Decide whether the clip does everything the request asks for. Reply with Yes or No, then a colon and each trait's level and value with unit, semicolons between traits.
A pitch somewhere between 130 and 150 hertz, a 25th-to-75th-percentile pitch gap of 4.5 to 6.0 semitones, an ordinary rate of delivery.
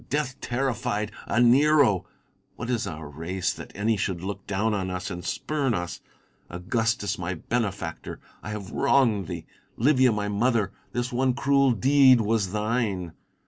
No: low, 110 Hz; average, 5.0 semitones; average, 155 wpm